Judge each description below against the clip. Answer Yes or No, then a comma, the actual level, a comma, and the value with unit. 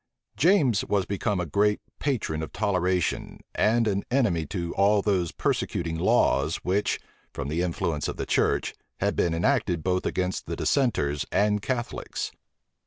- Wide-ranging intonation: No, average, 3.8 semitones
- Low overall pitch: Yes, very low, 95 Hz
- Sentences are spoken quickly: No, average, 150 wpm